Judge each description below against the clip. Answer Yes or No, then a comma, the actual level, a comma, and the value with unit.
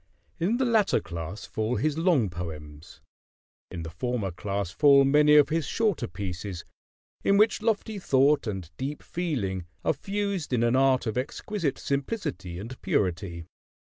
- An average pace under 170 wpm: Yes, average, 150 wpm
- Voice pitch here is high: No, low, 130 Hz